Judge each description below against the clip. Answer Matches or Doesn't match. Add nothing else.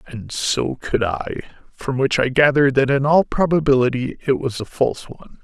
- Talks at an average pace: Matches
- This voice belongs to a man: Matches